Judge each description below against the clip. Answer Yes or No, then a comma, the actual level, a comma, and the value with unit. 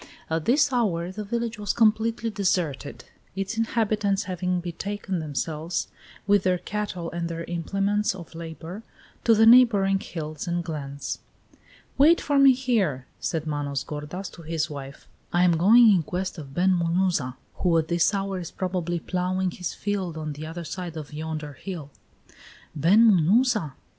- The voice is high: No, medium, 180 Hz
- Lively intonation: No, average, 4.1 semitones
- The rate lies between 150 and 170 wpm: Yes, average, 160 wpm